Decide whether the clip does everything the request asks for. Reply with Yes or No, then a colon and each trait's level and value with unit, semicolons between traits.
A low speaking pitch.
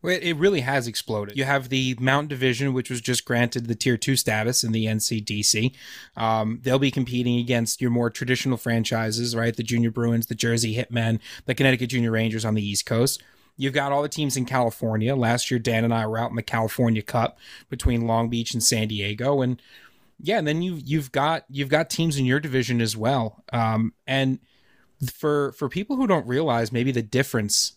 Yes: low, 125 Hz